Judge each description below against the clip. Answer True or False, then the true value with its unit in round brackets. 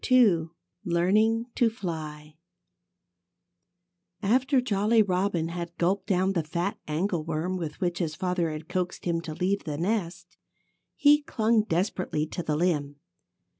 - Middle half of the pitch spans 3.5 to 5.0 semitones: True (3.9 semitones)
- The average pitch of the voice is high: False (180 Hz)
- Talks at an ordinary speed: False (130 wpm)